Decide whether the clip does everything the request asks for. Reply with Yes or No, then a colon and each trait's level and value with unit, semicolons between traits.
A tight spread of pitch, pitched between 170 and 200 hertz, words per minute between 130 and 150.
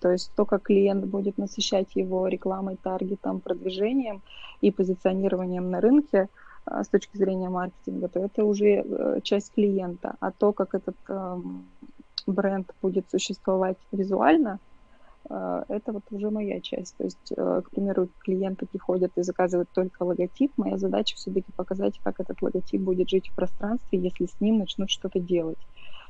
Yes: narrow, 1.9 semitones; high, 190 Hz; average, 145 wpm